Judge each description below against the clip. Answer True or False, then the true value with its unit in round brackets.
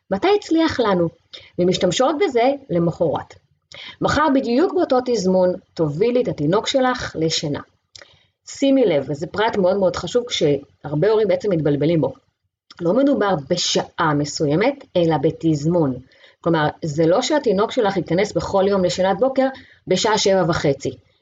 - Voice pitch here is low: False (180 Hz)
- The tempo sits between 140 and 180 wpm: False (130 wpm)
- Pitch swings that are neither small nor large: False (7.2 semitones)